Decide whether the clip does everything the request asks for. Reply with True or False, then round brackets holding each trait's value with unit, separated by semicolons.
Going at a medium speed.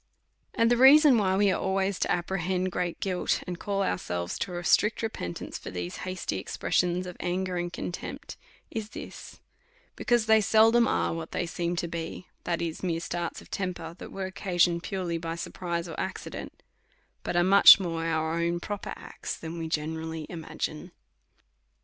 True (175 wpm)